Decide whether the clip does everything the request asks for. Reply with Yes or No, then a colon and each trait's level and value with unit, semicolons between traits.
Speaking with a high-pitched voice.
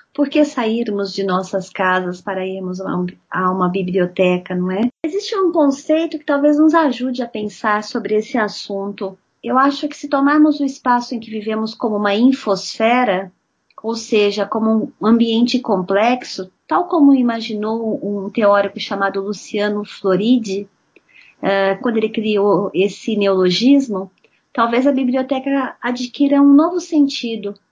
Yes: high, 220 Hz